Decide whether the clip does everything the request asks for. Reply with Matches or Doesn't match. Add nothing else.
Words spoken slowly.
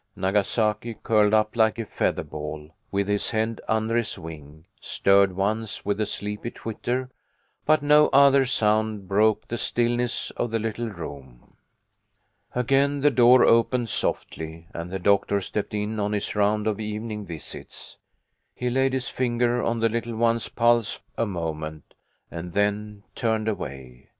Doesn't match